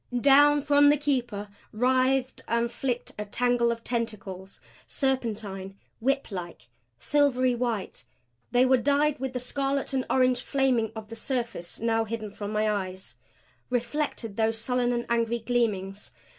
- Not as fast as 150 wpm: Yes, average, 140 wpm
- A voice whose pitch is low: No, high, 240 Hz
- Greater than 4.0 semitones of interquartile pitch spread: No, average, 3.4 semitones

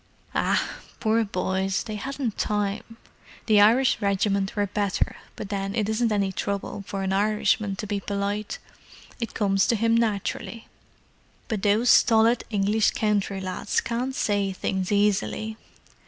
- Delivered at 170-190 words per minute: No, average, 140 wpm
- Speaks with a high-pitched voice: Yes, high, 205 Hz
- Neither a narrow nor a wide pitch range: No, narrow, 1.9 semitones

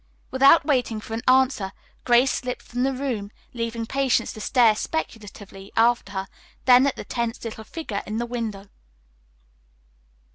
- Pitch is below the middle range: No, high, 235 Hz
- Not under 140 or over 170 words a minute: Yes, average, 150 wpm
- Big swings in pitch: No, average, 3.1 semitones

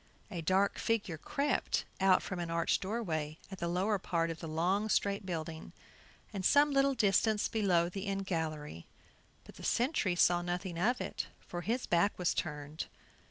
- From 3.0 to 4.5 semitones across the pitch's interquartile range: Yes, average, 3.7 semitones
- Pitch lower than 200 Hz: Yes, medium, 185 Hz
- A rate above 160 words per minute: Yes, average, 170 wpm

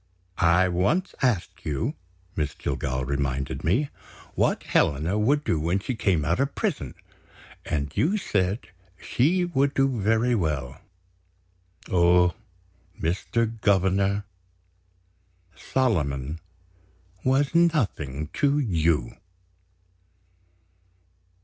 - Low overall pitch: Yes, very low, 95 Hz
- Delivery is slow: Yes, slow, 95 wpm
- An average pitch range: No, wide, 8.7 semitones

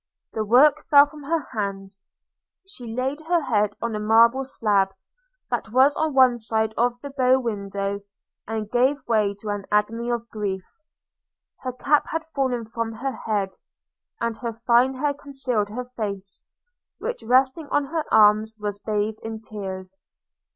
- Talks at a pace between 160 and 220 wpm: Yes, average, 165 wpm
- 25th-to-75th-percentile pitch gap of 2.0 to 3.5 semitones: No, average, 4.1 semitones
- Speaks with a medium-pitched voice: No, high, 230 Hz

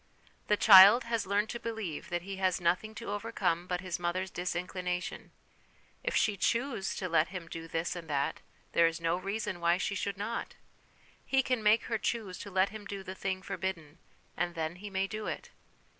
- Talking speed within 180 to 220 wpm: Yes, average, 195 wpm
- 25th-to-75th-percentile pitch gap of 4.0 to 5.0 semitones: No, average, 3.1 semitones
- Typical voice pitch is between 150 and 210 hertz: Yes, high, 190 Hz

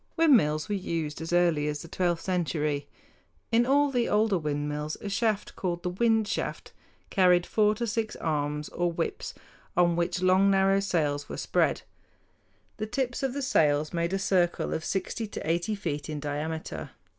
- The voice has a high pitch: No, medium, 175 Hz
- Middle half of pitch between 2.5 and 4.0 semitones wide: No, average, 5.3 semitones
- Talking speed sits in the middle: Yes, average, 170 wpm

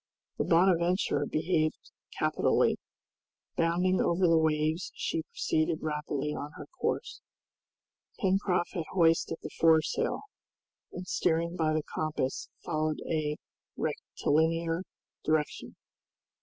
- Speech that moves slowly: Yes, slow, 100 wpm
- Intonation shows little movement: Yes, narrow, 1.9 semitones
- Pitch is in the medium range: Yes, medium, 165 Hz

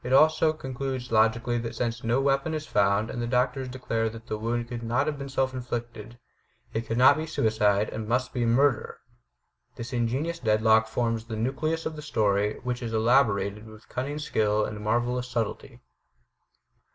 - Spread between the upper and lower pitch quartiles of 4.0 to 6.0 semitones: No, average, 2.9 semitones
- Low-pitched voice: Yes, low, 120 Hz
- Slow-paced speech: No, average, 175 wpm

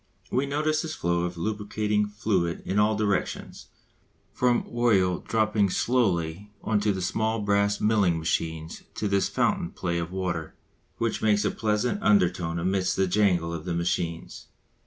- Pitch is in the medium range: No, low, 100 Hz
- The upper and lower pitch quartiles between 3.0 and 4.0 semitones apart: Yes, average, 3.7 semitones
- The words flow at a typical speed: Yes, average, 155 wpm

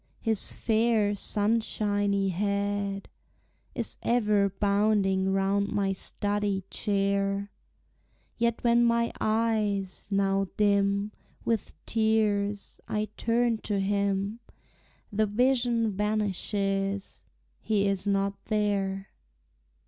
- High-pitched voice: Yes, high, 205 Hz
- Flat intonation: Yes, narrow, 1.7 semitones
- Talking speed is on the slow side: Yes, slow, 90 wpm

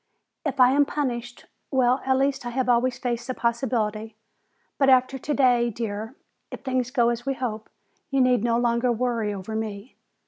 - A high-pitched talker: Yes, high, 245 Hz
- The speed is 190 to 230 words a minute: No, average, 175 wpm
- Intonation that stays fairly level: Yes, narrow, 2.0 semitones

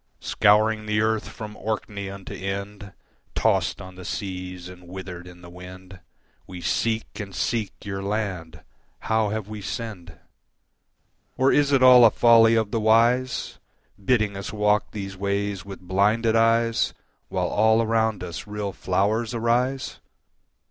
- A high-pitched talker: No, low, 105 Hz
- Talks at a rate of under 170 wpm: Yes, average, 145 wpm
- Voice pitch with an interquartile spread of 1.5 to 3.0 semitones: Yes, average, 2.7 semitones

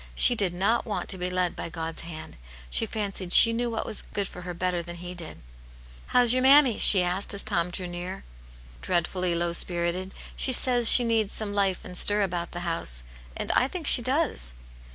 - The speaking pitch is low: No, medium, 185 Hz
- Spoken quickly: Yes, fast, 215 wpm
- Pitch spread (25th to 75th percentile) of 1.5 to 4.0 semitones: No, average, 4.4 semitones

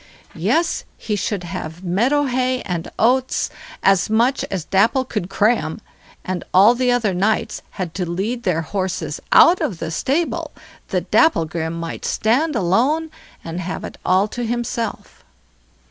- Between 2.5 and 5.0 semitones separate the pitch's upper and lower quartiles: No, wide, 5.5 semitones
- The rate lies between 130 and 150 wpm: Yes, average, 145 wpm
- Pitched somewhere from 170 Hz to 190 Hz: No, high, 210 Hz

